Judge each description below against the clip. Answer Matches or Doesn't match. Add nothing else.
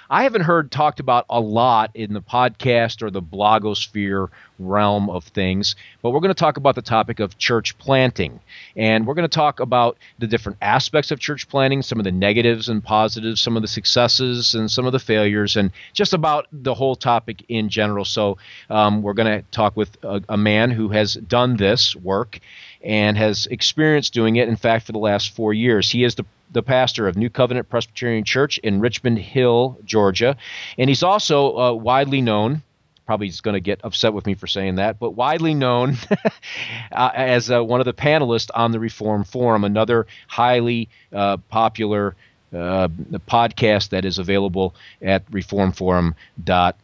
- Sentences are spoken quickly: Doesn't match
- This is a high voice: Doesn't match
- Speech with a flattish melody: Doesn't match